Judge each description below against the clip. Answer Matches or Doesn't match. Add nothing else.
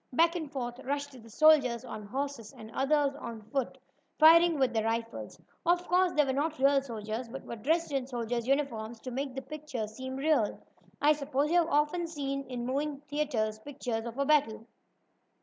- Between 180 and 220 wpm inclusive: Matches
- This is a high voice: Matches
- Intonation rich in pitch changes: Doesn't match